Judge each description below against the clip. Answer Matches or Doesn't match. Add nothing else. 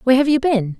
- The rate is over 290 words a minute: Matches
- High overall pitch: Matches